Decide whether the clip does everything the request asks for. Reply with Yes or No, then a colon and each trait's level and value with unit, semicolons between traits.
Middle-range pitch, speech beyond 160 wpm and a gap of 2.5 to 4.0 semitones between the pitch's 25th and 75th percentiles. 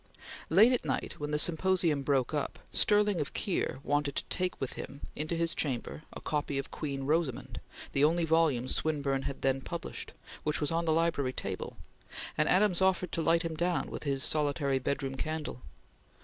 Yes: medium, 155 Hz; average, 180 wpm; average, 3.4 semitones